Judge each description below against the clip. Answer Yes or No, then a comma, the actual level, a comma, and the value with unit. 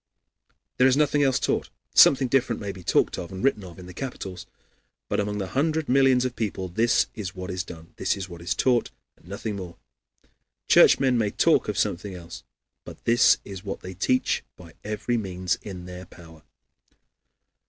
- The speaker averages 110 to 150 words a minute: No, average, 190 wpm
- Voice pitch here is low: Yes, low, 100 Hz